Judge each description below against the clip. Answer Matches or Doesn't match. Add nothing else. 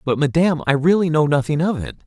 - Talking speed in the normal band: Doesn't match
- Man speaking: Matches